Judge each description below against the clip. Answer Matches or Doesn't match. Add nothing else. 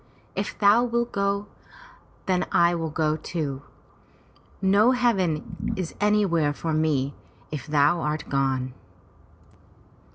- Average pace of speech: Doesn't match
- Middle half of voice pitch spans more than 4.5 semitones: Matches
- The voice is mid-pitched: Matches